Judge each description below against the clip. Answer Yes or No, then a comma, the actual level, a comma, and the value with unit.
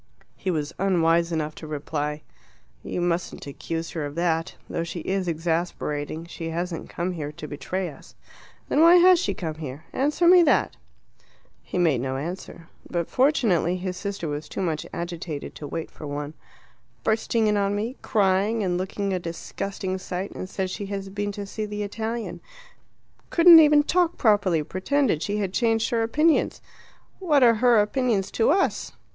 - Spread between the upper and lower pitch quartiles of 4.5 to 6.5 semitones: Yes, average, 5.1 semitones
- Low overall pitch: No, medium, 185 Hz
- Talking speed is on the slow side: No, average, 170 wpm